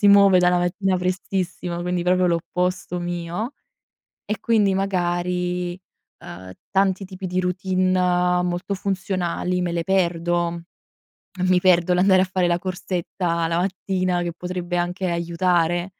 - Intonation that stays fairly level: Yes, narrow, 1.2 semitones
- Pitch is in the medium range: Yes, medium, 180 Hz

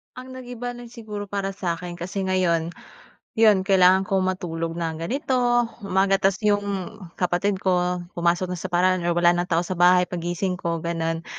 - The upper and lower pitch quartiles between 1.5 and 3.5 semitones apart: Yes, narrow, 2.6 semitones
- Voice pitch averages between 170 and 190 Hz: Yes, medium, 185 Hz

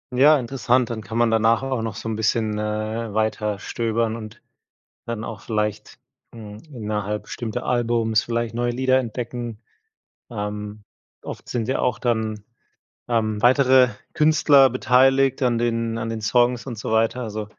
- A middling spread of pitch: No, narrow, 2.2 semitones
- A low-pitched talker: Yes, low, 115 Hz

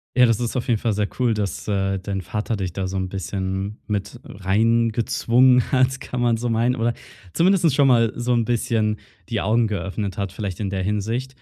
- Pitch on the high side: No, low, 110 Hz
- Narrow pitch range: No, average, 3.5 semitones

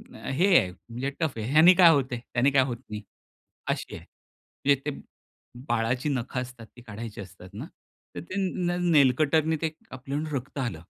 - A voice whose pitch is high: No, low, 130 Hz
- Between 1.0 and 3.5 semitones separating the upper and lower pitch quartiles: No, average, 4.2 semitones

